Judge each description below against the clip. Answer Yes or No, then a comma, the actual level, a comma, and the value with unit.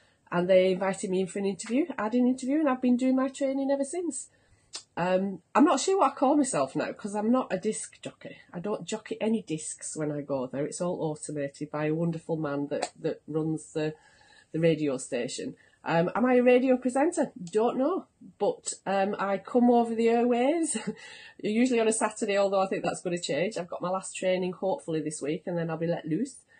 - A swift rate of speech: Yes, fast, 220 wpm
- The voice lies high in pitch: Yes, high, 205 Hz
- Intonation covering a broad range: Yes, wide, 7.3 semitones